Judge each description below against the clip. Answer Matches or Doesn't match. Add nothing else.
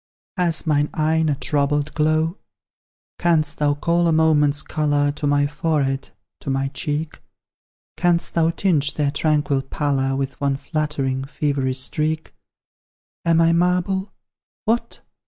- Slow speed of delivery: Matches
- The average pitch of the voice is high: Doesn't match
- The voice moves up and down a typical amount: Doesn't match